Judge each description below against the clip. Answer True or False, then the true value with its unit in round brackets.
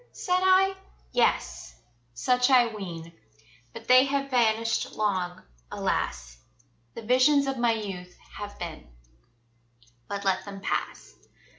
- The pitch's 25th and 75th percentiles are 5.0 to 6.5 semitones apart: True (5.5 semitones)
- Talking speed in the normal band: False (120 wpm)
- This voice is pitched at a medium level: False (220 Hz)